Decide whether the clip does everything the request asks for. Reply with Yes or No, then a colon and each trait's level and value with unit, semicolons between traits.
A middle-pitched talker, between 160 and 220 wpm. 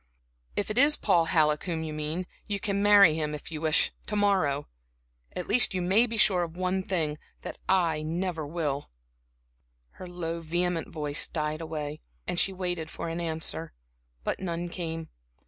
Yes: medium, 170 Hz; average, 175 wpm